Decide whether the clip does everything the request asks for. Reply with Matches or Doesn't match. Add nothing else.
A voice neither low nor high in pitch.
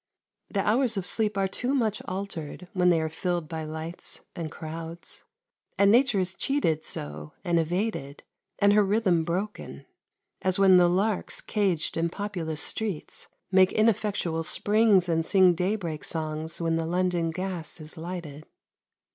Matches